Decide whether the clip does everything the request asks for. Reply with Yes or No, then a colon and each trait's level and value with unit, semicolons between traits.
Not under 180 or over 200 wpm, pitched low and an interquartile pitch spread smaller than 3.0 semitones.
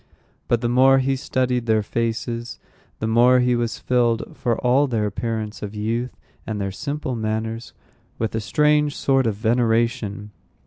No: average, 155 wpm; low, 115 Hz; narrow, 2.4 semitones